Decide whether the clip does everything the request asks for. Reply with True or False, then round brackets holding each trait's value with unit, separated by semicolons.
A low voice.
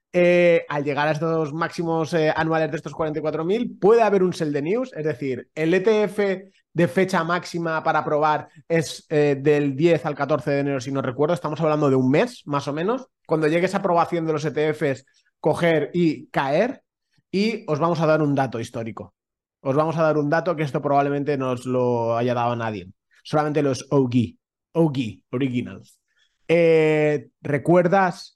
False (155 Hz)